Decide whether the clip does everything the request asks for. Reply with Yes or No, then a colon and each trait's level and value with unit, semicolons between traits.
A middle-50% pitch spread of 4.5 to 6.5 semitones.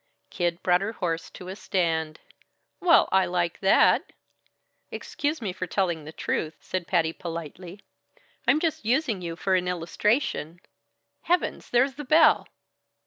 Yes: average, 5.2 semitones